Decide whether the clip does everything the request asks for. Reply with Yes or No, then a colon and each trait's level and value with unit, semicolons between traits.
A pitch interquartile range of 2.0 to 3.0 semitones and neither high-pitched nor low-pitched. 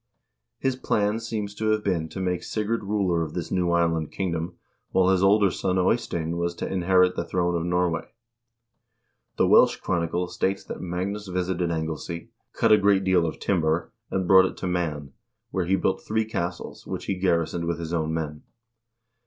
No: narrow, 2.4 semitones; very low, 90 Hz